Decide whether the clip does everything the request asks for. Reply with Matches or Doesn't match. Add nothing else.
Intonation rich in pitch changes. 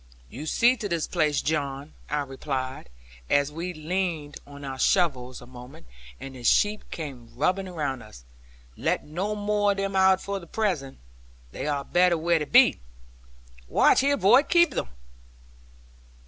Matches